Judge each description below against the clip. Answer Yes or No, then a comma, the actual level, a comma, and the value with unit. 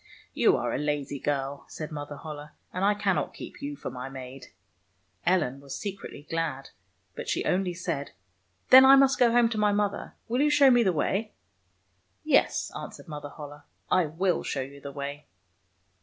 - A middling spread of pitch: No, wide, 6.4 semitones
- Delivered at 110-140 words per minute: No, average, 200 wpm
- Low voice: No, medium, 150 Hz